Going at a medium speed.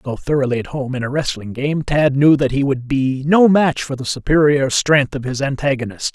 No: fast, 225 wpm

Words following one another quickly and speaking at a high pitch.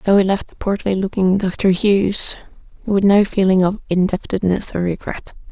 No: average, 165 wpm; high, 195 Hz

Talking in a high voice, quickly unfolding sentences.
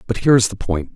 No: low, 105 Hz; fast, 315 wpm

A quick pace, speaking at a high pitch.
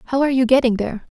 Yes: fast, 260 wpm; high, 245 Hz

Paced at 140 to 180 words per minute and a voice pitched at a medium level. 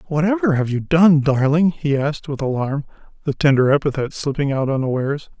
Yes: average, 165 wpm; medium, 145 Hz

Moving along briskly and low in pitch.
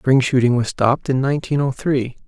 Yes: fast, 210 wpm; low, 130 Hz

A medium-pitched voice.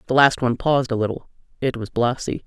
No: low, 125 Hz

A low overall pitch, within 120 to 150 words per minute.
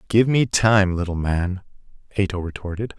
Yes: low, 100 Hz; average, 140 wpm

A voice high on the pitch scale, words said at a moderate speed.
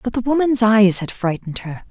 No: high, 215 Hz; fast, 220 wpm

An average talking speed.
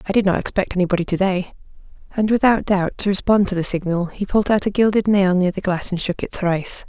No: fast, 245 wpm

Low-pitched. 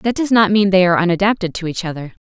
No: high, 190 Hz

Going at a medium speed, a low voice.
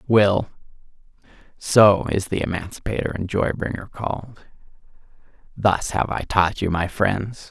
No: slow, 120 wpm; low, 100 Hz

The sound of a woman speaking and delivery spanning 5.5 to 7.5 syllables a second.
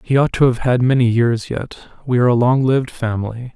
No: male; 5.8 syllables/s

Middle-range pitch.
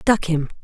Yes: medium, 175 Hz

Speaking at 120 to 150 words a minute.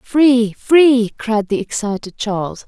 Yes: slow, 135 wpm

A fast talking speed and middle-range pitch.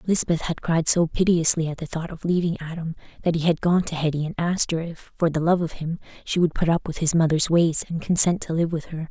Yes: fast, 265 wpm; medium, 165 Hz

